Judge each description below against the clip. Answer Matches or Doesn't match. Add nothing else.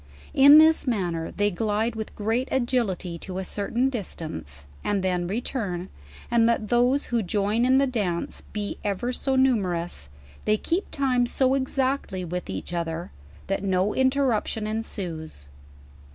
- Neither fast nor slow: Matches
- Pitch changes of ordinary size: Doesn't match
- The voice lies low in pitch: Doesn't match